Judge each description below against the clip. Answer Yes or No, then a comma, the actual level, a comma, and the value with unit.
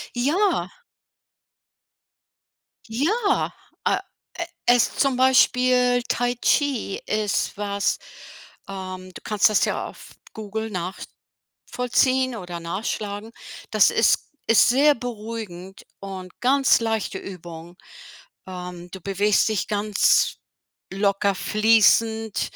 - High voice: Yes, high, 215 Hz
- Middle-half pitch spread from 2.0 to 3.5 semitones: No, average, 4.1 semitones